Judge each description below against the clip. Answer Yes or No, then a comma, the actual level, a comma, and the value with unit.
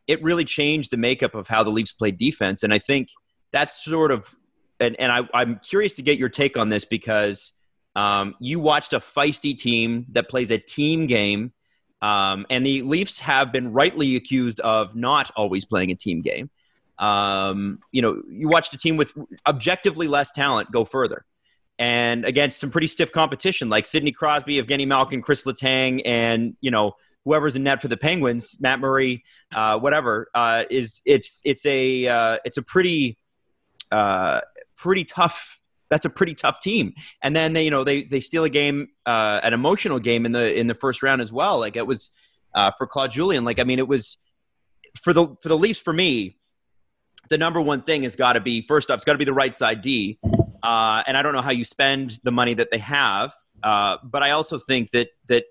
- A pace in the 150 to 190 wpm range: No, average, 200 wpm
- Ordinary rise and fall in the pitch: Yes, average, 4.1 semitones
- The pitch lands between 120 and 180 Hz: Yes, low, 135 Hz